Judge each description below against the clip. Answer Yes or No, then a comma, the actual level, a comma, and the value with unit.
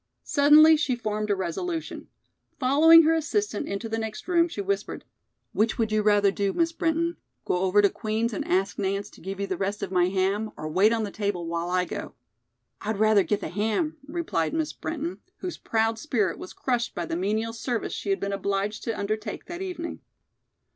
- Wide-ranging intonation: Yes, wide, 6.8 semitones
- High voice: Yes, high, 215 Hz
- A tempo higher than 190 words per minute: Yes, average, 200 wpm